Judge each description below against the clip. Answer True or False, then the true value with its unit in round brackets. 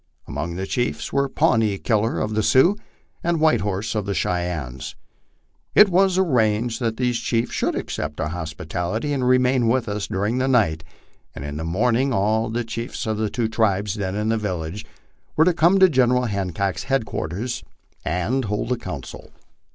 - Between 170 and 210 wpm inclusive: True (175 wpm)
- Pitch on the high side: False (110 Hz)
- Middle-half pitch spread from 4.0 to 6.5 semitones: True (4.9 semitones)